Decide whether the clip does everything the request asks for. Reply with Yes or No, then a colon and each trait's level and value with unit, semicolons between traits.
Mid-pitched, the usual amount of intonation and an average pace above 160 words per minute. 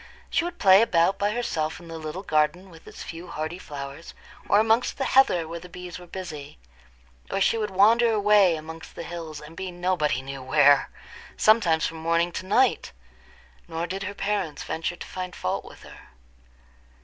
Yes: medium, 175 Hz; average, 3.8 semitones; average, 185 wpm